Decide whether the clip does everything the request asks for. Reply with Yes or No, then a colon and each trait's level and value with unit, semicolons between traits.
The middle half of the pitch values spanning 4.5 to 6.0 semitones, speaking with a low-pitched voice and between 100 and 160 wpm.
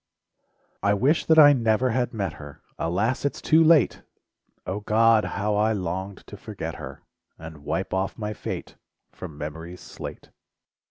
Yes: average, 5.1 semitones; low, 105 Hz; average, 155 wpm